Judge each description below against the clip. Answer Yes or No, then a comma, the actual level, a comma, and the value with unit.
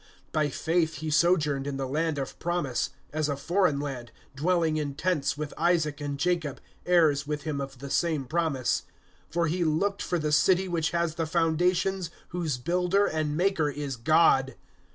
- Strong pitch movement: No, average, 3.3 semitones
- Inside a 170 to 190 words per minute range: Yes, average, 175 wpm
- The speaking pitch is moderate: Yes, medium, 155 Hz